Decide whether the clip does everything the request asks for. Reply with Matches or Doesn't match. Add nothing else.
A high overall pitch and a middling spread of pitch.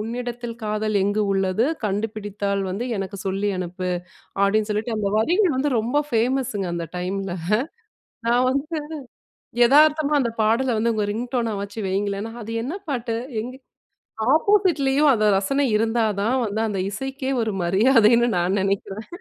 Matches